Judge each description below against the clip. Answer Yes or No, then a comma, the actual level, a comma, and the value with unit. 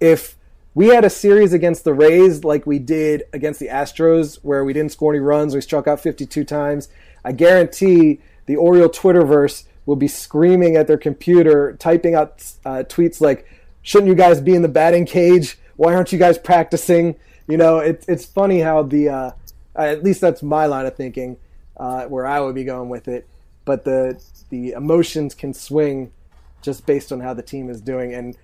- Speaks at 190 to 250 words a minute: Yes, average, 195 wpm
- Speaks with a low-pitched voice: No, medium, 150 Hz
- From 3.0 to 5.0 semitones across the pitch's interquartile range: Yes, average, 3.8 semitones